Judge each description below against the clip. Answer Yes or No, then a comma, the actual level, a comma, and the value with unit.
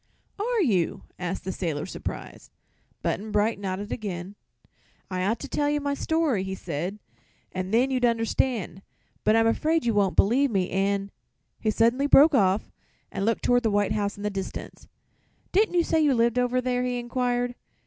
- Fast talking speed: No, average, 180 wpm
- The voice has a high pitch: Yes, high, 225 Hz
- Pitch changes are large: No, average, 4.5 semitones